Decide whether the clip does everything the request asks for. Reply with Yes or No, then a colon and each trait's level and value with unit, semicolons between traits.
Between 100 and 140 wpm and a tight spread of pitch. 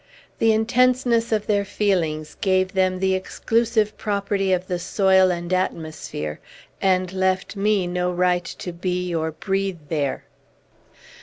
Yes: slow, 135 wpm; narrow, 2.3 semitones